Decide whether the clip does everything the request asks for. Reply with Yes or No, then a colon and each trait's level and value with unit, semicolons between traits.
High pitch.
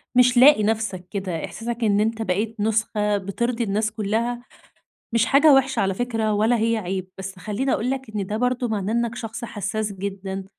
Yes: high, 220 Hz